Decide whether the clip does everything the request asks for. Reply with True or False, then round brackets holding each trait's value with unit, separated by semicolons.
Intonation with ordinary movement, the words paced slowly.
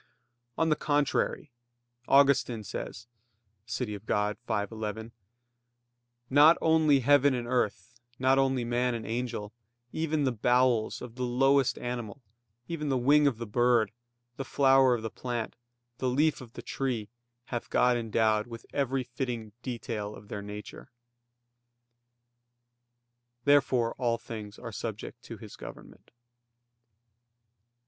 True (3.3 semitones; 130 wpm)